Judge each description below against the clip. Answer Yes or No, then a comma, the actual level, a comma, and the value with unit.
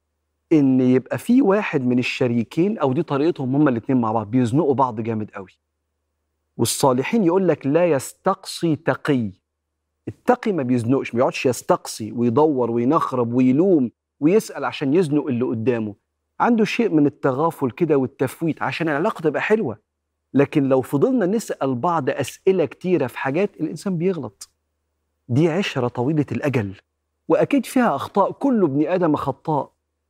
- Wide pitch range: Yes, wide, 6.3 semitones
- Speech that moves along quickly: Yes, fast, 140 wpm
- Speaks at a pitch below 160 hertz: Yes, low, 135 Hz